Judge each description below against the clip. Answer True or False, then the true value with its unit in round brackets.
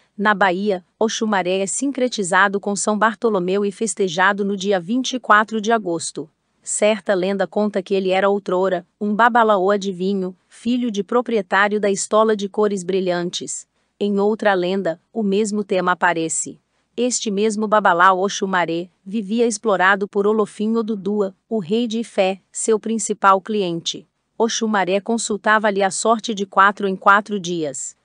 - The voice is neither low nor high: False (205 Hz)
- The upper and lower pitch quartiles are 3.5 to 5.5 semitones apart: False (2.4 semitones)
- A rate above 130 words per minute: True (140 wpm)